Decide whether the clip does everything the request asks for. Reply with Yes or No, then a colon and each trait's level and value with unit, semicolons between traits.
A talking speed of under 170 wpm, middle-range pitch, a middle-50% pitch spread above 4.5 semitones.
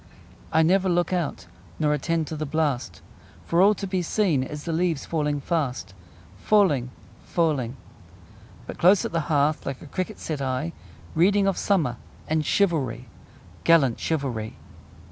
No: average, 150 wpm; medium, 160 Hz; average, 4.1 semitones